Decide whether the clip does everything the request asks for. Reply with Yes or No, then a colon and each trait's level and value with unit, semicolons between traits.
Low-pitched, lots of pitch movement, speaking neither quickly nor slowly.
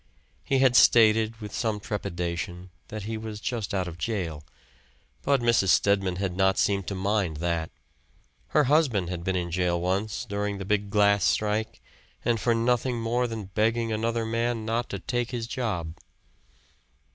No: low, 105 Hz; average, 3.6 semitones; average, 165 wpm